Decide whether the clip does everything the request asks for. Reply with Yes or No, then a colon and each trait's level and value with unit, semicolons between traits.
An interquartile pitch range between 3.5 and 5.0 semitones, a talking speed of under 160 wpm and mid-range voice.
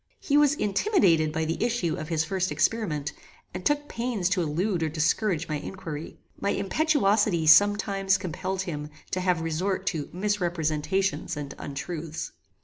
Yes: average, 4.2 semitones; average, 150 wpm; medium, 180 Hz